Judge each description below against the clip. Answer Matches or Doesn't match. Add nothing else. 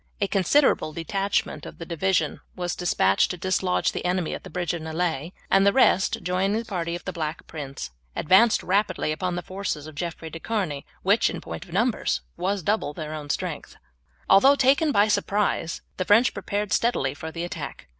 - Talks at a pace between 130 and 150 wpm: Doesn't match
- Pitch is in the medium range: Matches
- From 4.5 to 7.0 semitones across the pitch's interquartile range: Doesn't match